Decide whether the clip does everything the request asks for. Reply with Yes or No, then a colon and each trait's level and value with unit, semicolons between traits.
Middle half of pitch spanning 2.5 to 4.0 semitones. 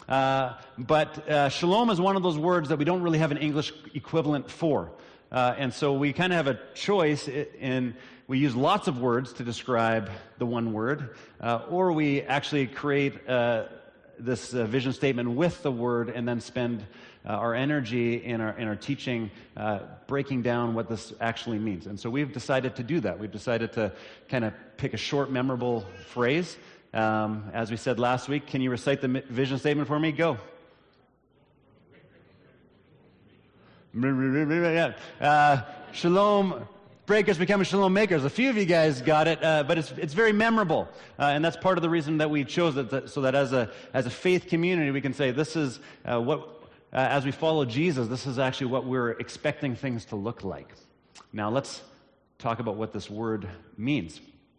No: average, 4.4 semitones